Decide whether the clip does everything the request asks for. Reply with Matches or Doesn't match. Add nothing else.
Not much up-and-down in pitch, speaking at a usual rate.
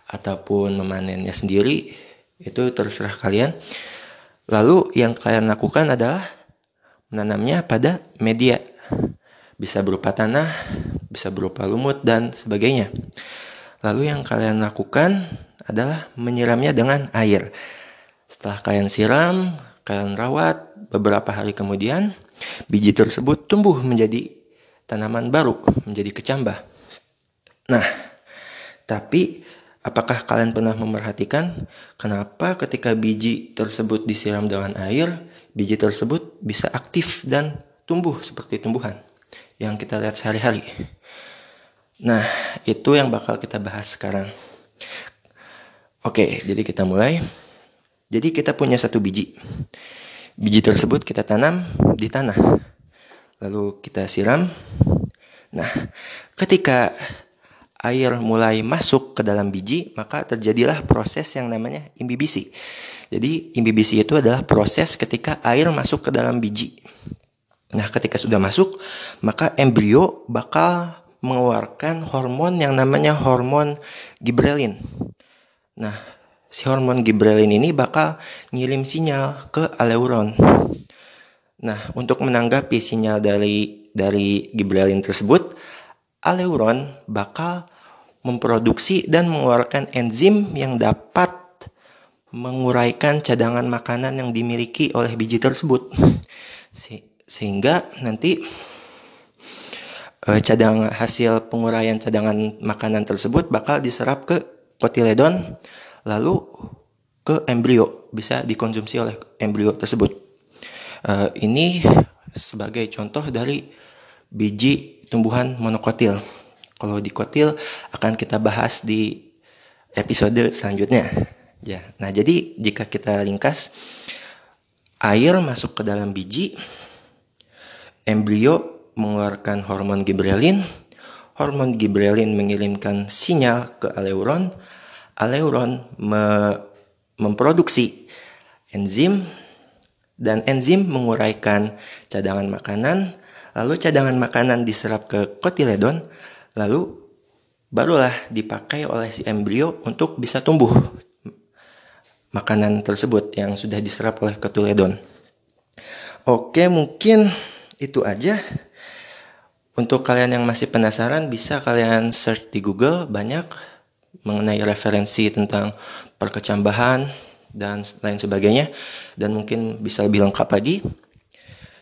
Doesn't match